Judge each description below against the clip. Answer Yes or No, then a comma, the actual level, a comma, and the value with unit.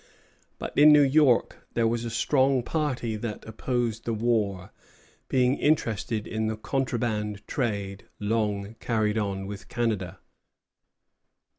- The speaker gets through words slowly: Yes, slow, 125 wpm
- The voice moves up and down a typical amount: Yes, average, 3.0 semitones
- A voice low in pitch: Yes, low, 115 Hz